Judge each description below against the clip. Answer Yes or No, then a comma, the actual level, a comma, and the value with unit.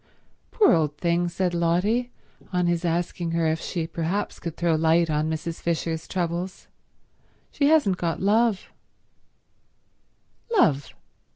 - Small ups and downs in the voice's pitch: Yes, narrow, 2.1 semitones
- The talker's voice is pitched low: No, medium, 170 Hz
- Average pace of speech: No, slow, 120 wpm